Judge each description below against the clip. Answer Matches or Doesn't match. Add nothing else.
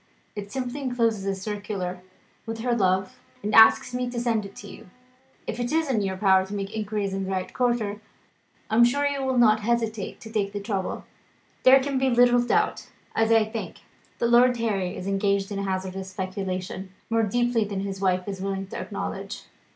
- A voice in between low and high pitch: Doesn't match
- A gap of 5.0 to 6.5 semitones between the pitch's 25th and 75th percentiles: Doesn't match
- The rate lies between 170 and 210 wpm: Matches